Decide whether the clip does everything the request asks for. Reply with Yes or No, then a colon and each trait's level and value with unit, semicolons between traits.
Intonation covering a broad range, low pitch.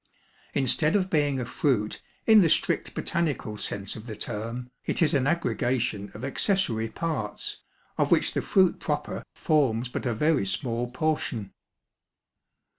Yes: wide, 5.9 semitones; low, 130 Hz